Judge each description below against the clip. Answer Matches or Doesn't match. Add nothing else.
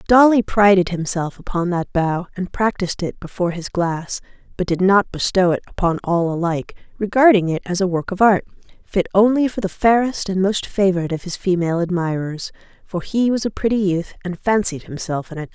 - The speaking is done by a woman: Matches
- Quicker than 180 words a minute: Matches